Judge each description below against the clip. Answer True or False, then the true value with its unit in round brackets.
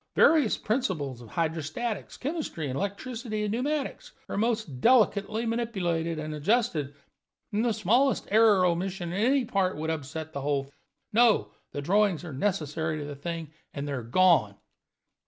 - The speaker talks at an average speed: True (155 wpm)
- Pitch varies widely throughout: True (6.6 semitones)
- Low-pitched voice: False (185 Hz)